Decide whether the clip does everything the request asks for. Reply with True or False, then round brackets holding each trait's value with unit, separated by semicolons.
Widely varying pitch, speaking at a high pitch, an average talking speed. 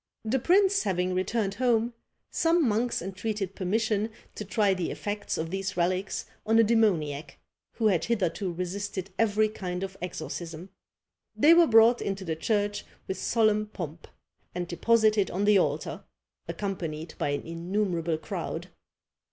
False (3.6 semitones; 200 Hz; 145 wpm)